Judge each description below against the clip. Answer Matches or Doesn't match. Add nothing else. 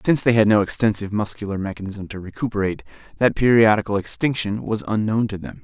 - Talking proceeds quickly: Doesn't match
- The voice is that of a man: Matches